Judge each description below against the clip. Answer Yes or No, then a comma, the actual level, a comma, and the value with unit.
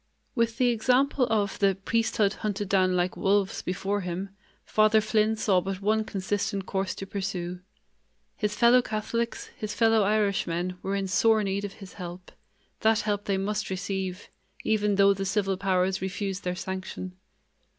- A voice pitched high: Yes, high, 200 Hz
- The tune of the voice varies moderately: No, narrow, 2.2 semitones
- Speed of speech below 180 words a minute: Yes, average, 160 wpm